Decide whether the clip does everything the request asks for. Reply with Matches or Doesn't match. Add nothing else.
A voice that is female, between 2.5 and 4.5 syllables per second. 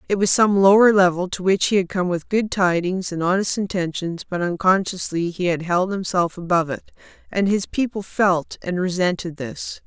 Doesn't match